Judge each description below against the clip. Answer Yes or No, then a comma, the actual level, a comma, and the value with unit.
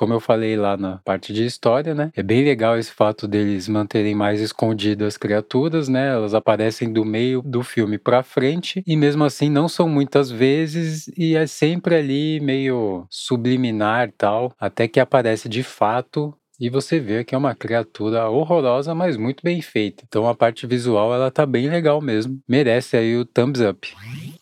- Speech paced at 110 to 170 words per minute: No, average, 180 wpm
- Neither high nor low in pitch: No, low, 125 Hz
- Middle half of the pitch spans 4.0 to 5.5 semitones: Yes, average, 4.7 semitones